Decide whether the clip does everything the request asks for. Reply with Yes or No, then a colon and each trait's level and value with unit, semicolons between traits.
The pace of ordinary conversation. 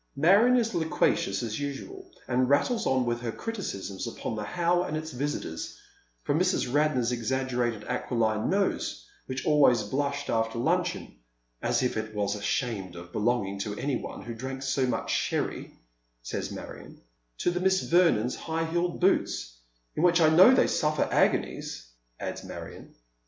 Yes: average, 160 wpm